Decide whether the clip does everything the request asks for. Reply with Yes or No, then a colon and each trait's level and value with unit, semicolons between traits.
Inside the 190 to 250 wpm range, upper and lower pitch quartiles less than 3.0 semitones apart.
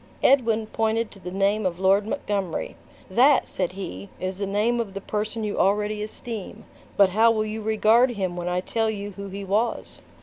Yes: average, 195 wpm; narrow, 2.4 semitones